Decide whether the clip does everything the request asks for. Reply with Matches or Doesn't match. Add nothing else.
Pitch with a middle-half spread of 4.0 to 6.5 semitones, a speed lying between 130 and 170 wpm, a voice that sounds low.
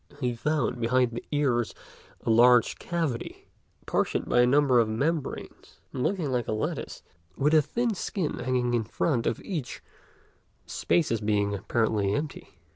Matches